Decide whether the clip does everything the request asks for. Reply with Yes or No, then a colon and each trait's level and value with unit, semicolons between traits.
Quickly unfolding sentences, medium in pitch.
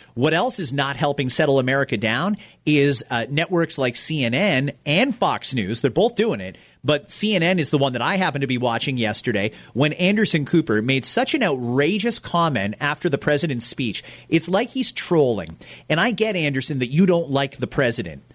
No: average, 190 wpm; medium, 145 Hz